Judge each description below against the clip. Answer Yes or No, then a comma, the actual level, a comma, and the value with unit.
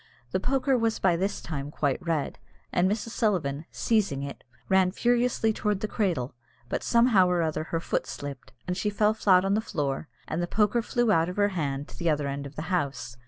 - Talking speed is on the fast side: Yes, fast, 215 wpm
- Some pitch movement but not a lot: No, wide, 6.1 semitones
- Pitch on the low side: No, medium, 180 Hz